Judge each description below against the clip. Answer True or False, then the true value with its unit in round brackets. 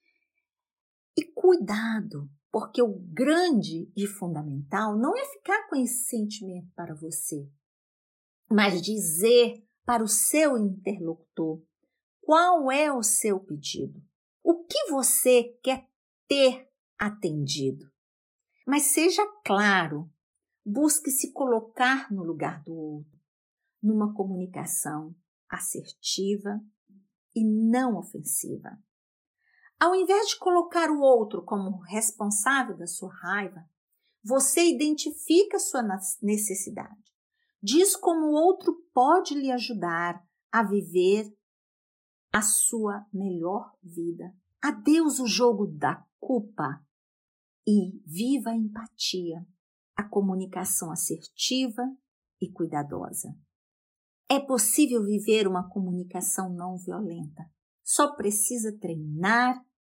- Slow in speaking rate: True (100 wpm)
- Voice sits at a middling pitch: False (215 Hz)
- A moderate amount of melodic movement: False (6.7 semitones)